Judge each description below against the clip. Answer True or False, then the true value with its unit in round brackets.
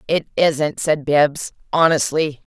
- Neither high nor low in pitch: True (150 Hz)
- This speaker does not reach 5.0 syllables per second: True (3.6 syllables/s)